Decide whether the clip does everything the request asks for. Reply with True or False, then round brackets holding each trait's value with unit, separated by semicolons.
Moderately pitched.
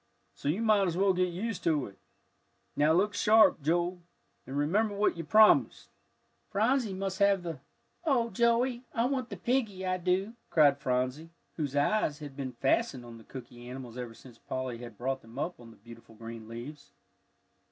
True (165 Hz)